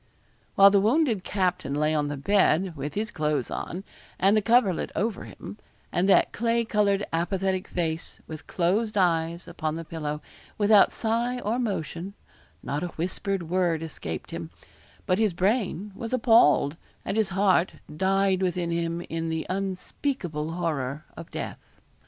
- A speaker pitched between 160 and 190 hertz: Yes, medium, 185 Hz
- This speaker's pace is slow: No, average, 150 wpm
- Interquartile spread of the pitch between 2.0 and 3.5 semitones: No, average, 4.0 semitones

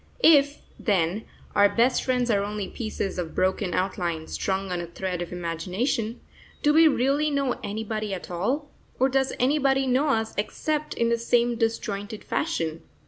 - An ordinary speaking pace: Yes, average, 160 wpm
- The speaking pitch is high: Yes, high, 220 Hz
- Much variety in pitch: Yes, wide, 5.9 semitones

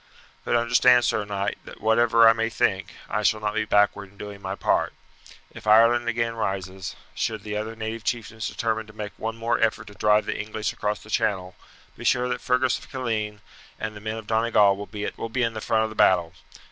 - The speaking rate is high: Yes, fast, 210 wpm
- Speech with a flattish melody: Yes, narrow, 1.8 semitones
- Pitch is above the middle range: No, low, 110 Hz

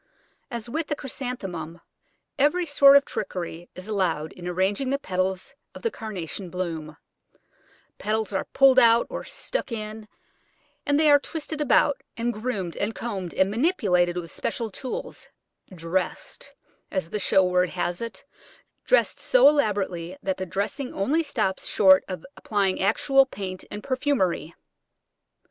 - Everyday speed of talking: Yes, average, 145 wpm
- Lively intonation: Yes, wide, 6.5 semitones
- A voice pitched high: Yes, high, 205 Hz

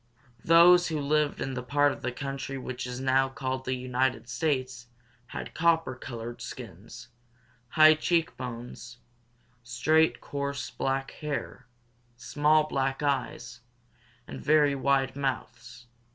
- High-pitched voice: No, low, 135 Hz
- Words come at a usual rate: No, slow, 125 wpm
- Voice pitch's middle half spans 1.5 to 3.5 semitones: Yes, average, 2.9 semitones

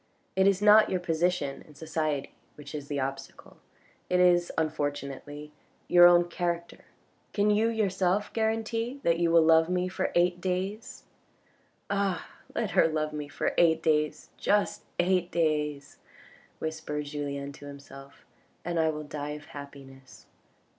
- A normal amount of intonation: Yes, average, 3.6 semitones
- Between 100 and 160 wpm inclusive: Yes, average, 150 wpm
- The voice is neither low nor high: Yes, medium, 160 Hz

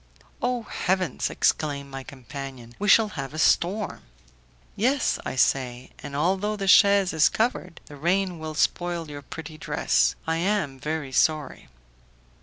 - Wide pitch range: Yes, wide, 5.8 semitones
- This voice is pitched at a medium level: Yes, medium, 160 Hz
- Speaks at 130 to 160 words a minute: Yes, average, 145 wpm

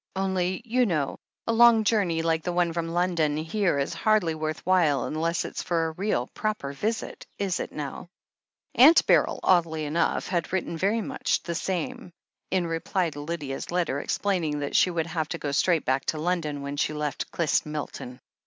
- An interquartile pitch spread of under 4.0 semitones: Yes, average, 3.6 semitones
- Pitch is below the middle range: No, medium, 170 Hz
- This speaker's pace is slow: No, average, 185 wpm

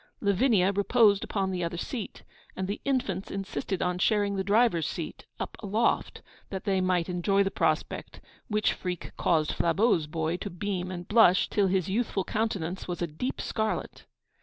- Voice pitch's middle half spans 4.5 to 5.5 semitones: No, average, 2.8 semitones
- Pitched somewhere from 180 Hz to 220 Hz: Yes, high, 190 Hz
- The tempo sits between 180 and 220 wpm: No, average, 165 wpm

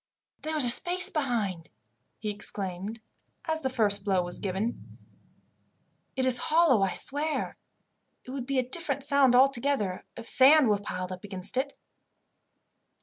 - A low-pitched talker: No, high, 245 Hz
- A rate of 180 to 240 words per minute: No, average, 145 wpm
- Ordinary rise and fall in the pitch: No, wide, 5.8 semitones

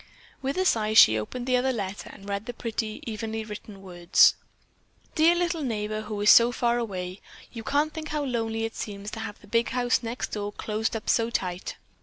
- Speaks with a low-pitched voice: No, high, 225 Hz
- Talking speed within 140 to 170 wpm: No, fast, 205 wpm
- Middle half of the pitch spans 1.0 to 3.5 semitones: Yes, average, 2.9 semitones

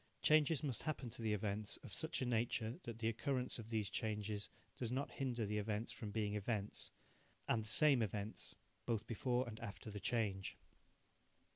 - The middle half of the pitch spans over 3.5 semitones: No, narrow, 2.6 semitones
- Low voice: Yes, low, 110 Hz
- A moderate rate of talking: Yes, average, 175 wpm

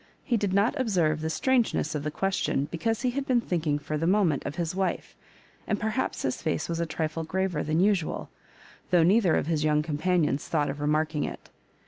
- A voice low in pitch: No, medium, 165 Hz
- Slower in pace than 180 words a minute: No, average, 195 wpm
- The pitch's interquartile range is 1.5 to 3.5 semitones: No, average, 4.6 semitones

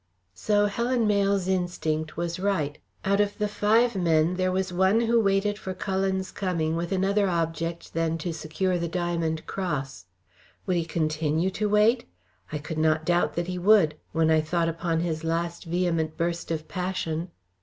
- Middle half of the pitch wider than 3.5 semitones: No, average, 3.2 semitones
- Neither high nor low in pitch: Yes, medium, 175 Hz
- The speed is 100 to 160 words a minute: No, average, 170 wpm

